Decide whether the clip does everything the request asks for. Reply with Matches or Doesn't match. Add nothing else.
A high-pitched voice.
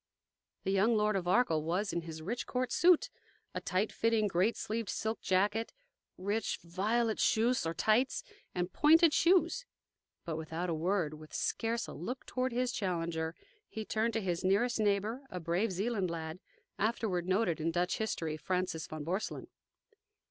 Matches